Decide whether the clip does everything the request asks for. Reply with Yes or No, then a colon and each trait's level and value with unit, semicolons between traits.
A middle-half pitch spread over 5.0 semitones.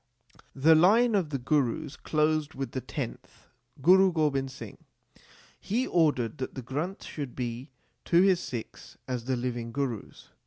No: average, 4.7 semitones